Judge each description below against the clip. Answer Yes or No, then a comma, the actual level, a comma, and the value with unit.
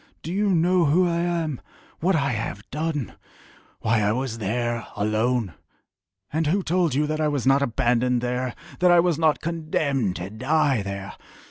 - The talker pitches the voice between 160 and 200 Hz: No, medium, 140 Hz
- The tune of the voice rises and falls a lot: Yes, wide, 5.9 semitones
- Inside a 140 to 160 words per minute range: No, average, 170 wpm